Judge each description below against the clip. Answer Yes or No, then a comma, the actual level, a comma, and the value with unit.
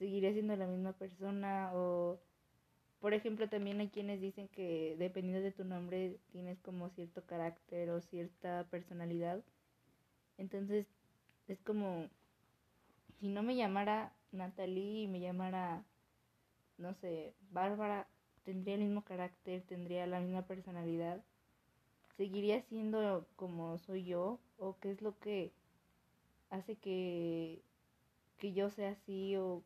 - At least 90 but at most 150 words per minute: Yes, slow, 125 wpm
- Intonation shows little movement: Yes, narrow, 2.1 semitones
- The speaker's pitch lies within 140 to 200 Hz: Yes, high, 190 Hz